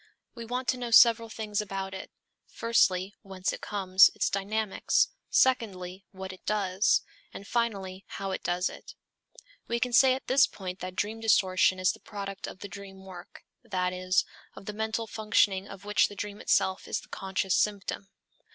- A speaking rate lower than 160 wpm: No, average, 180 wpm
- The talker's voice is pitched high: Yes, high, 195 Hz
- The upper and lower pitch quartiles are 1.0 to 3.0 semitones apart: Yes, average, 2.7 semitones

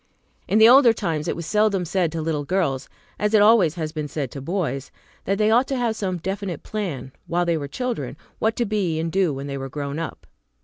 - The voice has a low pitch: No, medium, 175 Hz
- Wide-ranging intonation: Yes, wide, 5.7 semitones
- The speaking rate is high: Yes, fast, 230 wpm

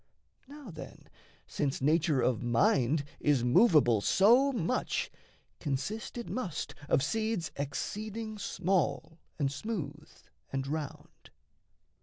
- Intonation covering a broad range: Yes, wide, 7.7 semitones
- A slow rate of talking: Yes, slow, 105 wpm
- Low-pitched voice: No, medium, 160 Hz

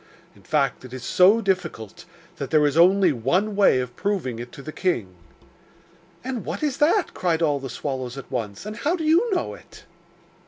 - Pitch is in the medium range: Yes, medium, 165 Hz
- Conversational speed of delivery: Yes, average, 195 wpm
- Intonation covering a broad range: Yes, wide, 8.4 semitones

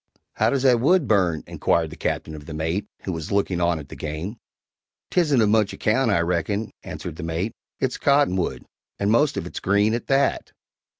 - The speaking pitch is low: Yes, low, 100 Hz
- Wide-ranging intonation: Yes, wide, 6.3 semitones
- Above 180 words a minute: Yes, average, 195 wpm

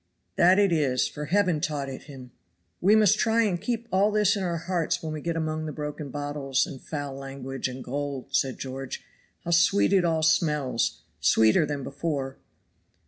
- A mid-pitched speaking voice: Yes, medium, 150 Hz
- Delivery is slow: No, average, 185 wpm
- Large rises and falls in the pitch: No, average, 4.3 semitones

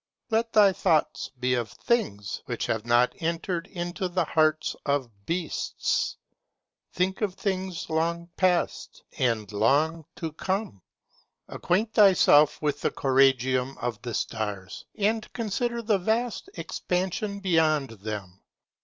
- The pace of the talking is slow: Yes, slow, 125 wpm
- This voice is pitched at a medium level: Yes, medium, 165 Hz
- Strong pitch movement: Yes, wide, 7.3 semitones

